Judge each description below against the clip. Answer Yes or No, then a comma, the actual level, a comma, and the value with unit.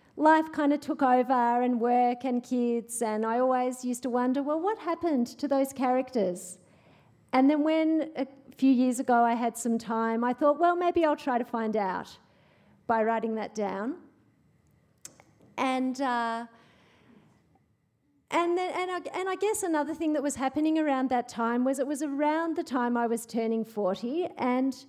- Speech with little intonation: No, average, 4.2 semitones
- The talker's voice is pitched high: Yes, very high, 255 Hz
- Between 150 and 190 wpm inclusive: Yes, average, 175 wpm